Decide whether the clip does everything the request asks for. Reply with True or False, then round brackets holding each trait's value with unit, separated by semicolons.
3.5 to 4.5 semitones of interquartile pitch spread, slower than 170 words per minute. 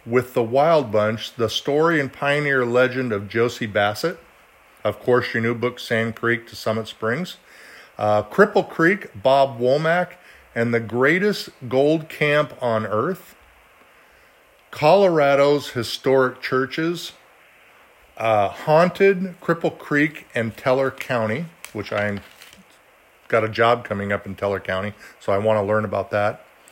False (5.5 semitones; 135 wpm)